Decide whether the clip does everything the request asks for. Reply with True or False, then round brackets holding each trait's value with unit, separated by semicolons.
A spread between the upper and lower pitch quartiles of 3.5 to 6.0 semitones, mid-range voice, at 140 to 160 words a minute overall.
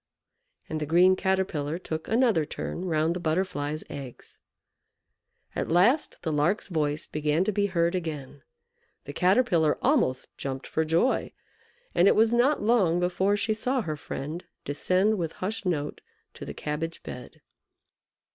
True (4.5 semitones; 175 Hz; 145 wpm)